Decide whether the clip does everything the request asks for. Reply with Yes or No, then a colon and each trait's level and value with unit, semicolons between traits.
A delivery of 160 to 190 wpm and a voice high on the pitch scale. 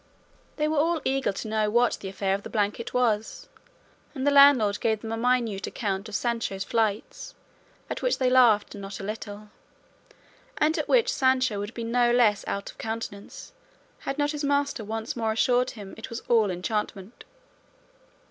Yes: average, 180 wpm; high, 225 Hz